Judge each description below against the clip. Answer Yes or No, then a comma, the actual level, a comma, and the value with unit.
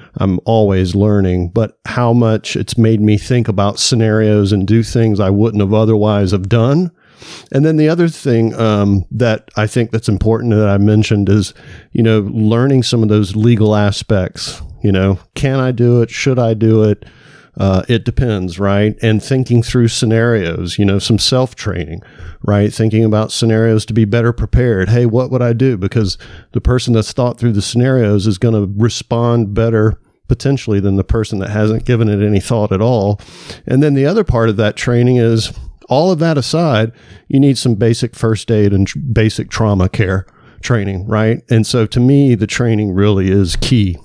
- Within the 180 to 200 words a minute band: Yes, average, 190 wpm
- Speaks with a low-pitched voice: Yes, low, 110 Hz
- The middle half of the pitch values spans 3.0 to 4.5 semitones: No, narrow, 2.6 semitones